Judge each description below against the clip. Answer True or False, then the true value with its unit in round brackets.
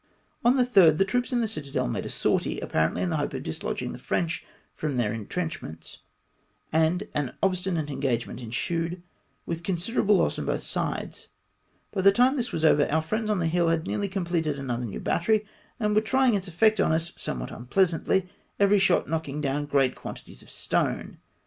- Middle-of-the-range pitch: True (170 Hz)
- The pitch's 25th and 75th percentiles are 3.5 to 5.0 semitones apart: False (5.5 semitones)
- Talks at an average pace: True (190 wpm)